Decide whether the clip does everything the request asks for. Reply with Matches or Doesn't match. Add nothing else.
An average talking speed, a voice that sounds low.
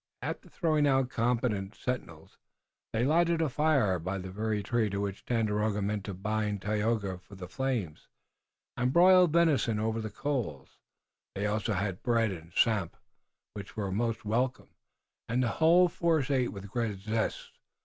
Matches